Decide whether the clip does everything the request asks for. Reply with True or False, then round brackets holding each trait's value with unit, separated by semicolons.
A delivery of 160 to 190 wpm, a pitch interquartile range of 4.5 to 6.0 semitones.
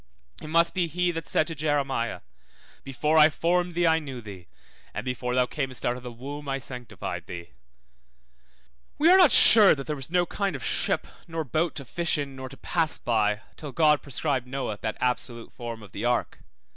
False (200 wpm; 4.9 semitones)